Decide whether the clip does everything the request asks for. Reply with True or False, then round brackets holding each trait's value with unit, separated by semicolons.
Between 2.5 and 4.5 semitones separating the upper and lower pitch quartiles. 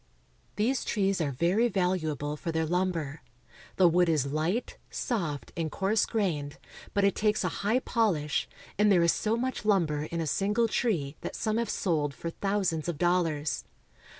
False (5.1 semitones)